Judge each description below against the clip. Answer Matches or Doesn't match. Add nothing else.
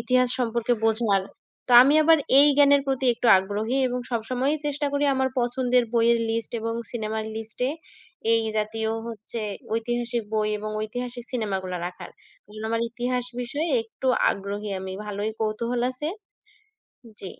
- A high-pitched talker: Matches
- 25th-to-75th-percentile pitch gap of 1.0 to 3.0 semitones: Matches